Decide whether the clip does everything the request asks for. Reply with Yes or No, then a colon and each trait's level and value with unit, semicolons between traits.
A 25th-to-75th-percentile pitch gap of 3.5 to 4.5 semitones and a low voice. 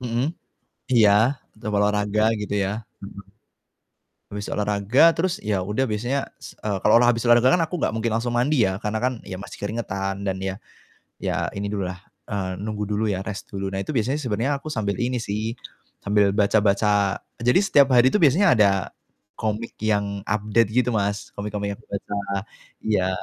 No: average, 3.0 semitones; low, 105 Hz